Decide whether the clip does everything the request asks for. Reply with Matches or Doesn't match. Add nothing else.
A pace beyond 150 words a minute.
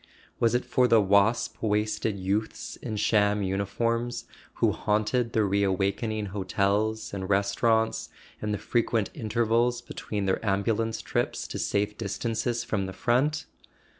Doesn't match